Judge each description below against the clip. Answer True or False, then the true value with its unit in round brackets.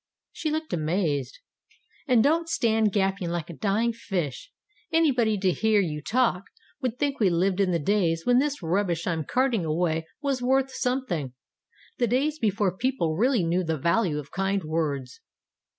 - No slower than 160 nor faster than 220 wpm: True (165 wpm)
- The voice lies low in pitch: False (195 Hz)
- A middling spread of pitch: False (7.0 semitones)